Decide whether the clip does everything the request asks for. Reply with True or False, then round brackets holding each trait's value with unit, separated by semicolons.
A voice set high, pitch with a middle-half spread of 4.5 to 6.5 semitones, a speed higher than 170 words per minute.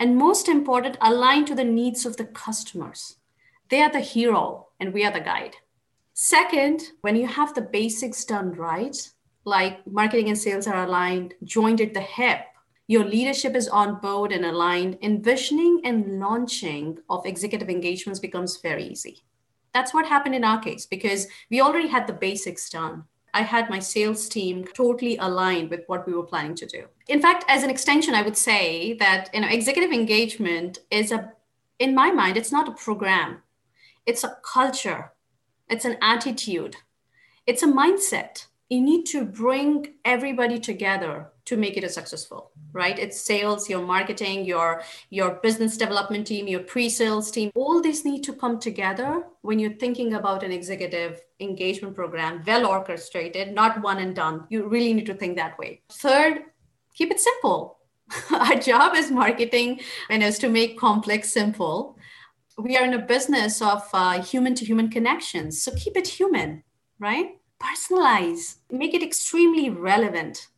False (220 Hz; 5.2 semitones; 165 wpm)